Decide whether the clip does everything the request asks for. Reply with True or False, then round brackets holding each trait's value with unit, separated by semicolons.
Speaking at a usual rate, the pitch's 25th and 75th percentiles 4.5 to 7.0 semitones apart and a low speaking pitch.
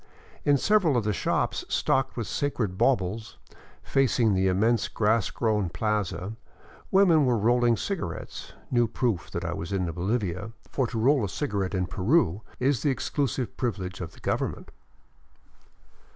True (150 wpm; 5.2 semitones; 110 Hz)